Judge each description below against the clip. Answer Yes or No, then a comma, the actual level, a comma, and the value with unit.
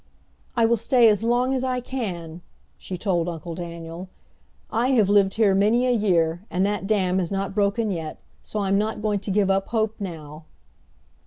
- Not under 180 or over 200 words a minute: Yes, average, 185 wpm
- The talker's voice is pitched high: Yes, high, 200 Hz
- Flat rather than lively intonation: No, average, 3.8 semitones